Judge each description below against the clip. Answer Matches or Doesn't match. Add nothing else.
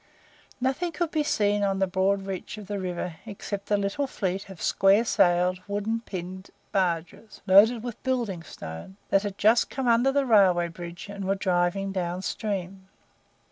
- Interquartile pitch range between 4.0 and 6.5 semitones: Doesn't match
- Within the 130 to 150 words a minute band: Doesn't match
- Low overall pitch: Doesn't match